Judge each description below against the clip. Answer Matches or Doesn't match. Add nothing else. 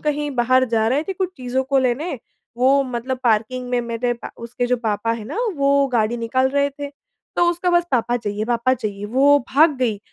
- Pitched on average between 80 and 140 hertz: Doesn't match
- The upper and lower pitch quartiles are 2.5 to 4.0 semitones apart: Matches